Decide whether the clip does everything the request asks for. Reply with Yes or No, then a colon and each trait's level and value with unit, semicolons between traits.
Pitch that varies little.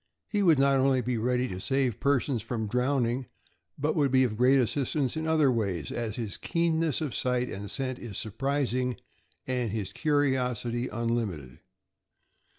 No: average, 3.1 semitones